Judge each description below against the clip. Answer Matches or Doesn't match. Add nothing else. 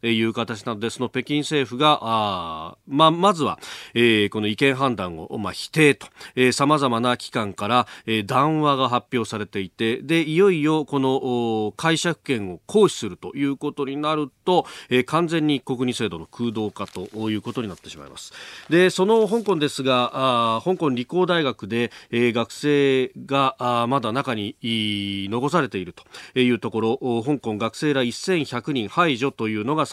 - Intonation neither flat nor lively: Matches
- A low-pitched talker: Matches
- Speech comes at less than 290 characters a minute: Doesn't match